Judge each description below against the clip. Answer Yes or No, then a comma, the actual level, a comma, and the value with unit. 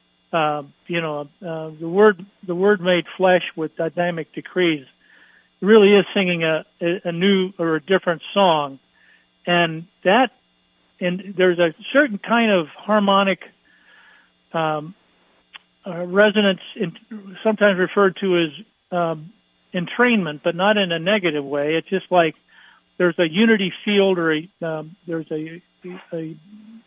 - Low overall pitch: No, medium, 180 Hz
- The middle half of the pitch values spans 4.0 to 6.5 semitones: No, average, 3.5 semitones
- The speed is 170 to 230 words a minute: No, average, 140 wpm